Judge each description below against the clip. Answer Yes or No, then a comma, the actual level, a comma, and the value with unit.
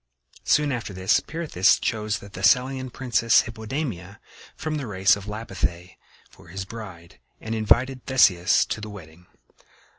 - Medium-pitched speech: No, low, 105 Hz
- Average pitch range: Yes, average, 5.0 semitones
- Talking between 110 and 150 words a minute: Yes, average, 140 wpm